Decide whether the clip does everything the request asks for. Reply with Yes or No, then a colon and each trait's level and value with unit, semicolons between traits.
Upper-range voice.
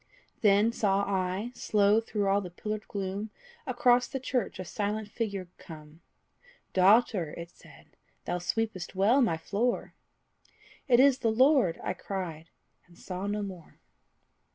Yes: high, 200 Hz